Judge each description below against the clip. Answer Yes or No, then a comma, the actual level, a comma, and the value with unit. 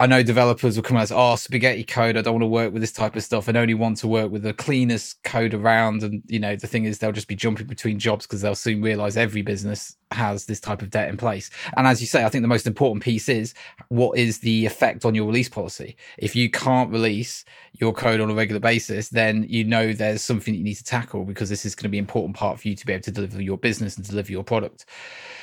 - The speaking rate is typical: No, fast, 270 wpm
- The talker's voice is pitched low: Yes, low, 110 Hz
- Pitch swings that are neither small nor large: No, narrow, 2.0 semitones